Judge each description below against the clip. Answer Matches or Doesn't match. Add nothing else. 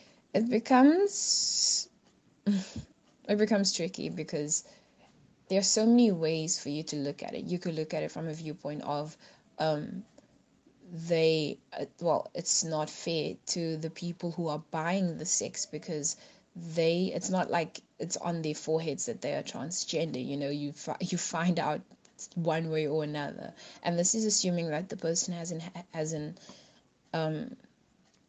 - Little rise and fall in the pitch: Doesn't match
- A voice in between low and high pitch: Matches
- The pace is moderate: Matches